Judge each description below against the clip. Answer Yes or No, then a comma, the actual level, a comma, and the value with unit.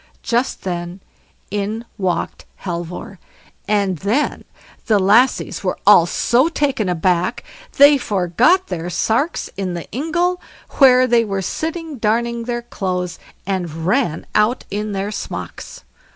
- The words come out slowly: Yes, slow, 125 wpm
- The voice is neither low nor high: No, high, 210 Hz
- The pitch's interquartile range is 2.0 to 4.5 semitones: No, wide, 5.6 semitones